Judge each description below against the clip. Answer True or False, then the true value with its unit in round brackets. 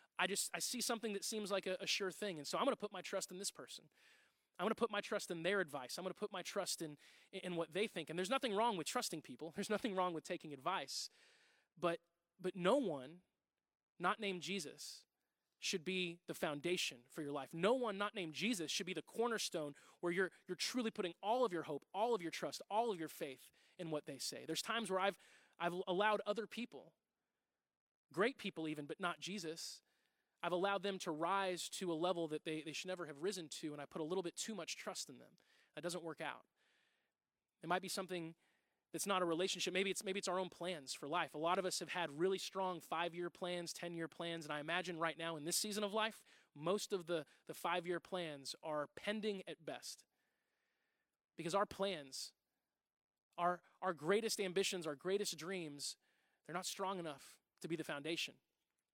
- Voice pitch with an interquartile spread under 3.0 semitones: False (3.4 semitones)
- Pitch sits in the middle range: True (180 Hz)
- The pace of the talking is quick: True (220 wpm)